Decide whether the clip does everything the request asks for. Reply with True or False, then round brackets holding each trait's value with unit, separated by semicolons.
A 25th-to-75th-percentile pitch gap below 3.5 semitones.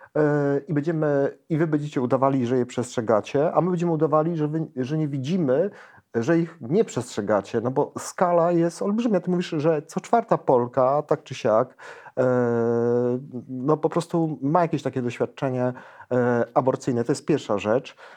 False (4.7 semitones)